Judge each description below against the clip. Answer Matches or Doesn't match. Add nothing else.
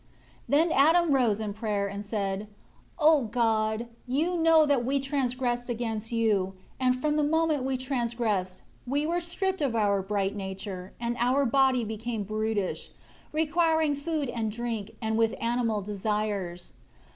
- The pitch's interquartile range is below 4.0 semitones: Doesn't match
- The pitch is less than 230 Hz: Doesn't match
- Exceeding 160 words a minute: Doesn't match